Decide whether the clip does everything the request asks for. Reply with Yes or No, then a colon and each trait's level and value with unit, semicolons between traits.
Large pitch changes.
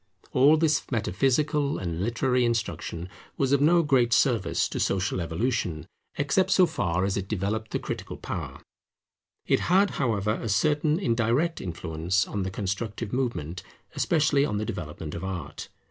Yes: wide, 7.2 semitones